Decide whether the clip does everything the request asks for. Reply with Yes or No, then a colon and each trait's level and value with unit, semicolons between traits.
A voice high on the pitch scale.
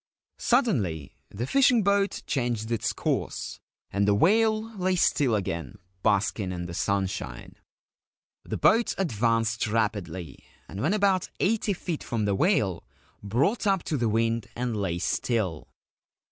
No: low, 115 Hz